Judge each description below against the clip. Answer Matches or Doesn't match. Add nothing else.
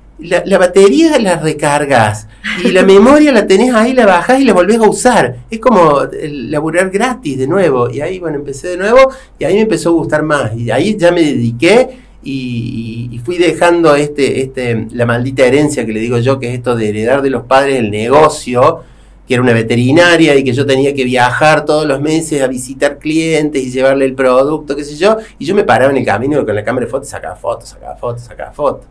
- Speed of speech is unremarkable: Doesn't match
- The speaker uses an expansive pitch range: Matches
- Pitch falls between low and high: Matches